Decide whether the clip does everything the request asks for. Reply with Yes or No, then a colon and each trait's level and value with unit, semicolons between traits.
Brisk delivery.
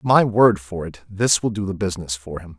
Yes: fast, 255 wpm